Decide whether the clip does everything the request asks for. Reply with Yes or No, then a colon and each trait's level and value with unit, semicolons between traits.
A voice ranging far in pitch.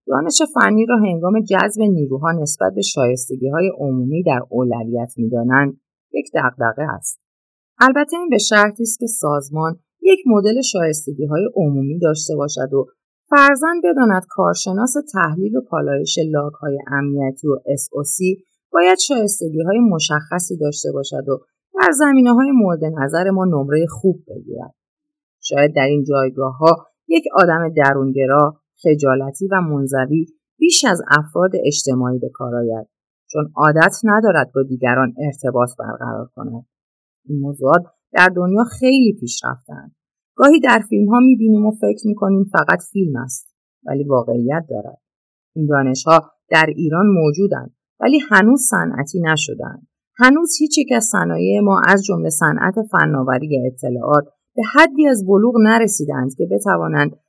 Yes: wide, 7.5 semitones